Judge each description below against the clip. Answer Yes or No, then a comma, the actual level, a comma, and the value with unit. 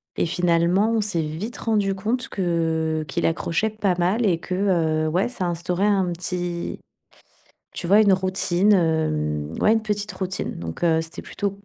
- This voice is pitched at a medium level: Yes, medium, 180 Hz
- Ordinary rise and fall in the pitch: Yes, average, 3.6 semitones